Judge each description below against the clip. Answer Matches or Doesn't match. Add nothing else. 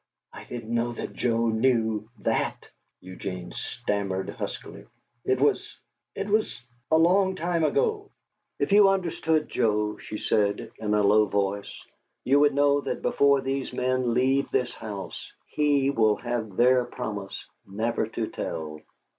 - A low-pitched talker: Matches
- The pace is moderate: Matches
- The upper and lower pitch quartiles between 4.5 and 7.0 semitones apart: Matches